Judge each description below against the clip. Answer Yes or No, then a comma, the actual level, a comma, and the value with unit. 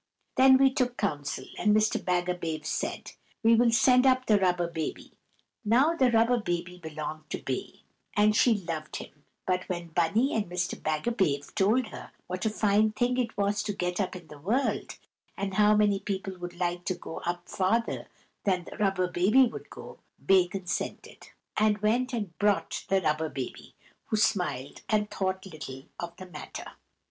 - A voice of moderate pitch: No, high, 195 Hz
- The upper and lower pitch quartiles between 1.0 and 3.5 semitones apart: No, average, 3.9 semitones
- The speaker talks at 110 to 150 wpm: No, average, 175 wpm